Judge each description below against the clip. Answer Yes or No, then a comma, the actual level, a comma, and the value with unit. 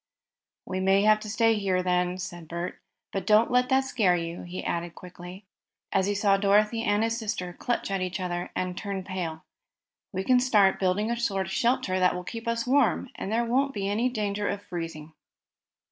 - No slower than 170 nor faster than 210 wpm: Yes, average, 190 wpm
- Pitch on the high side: Yes, high, 195 Hz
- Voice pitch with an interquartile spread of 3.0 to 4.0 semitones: Yes, average, 3.7 semitones